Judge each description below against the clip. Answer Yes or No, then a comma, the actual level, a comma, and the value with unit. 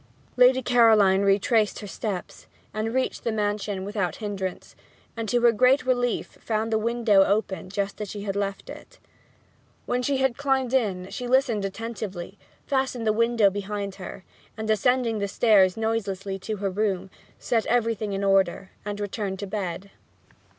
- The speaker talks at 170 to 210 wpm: No, average, 160 wpm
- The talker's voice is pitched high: Yes, high, 210 Hz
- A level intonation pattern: No, average, 3.1 semitones